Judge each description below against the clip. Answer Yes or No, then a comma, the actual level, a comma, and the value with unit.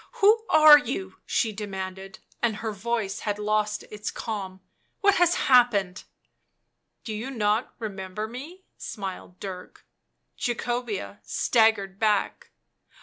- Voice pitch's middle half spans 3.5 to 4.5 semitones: Yes, average, 3.8 semitones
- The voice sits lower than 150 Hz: No, high, 215 Hz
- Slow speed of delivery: Yes, slow, 130 wpm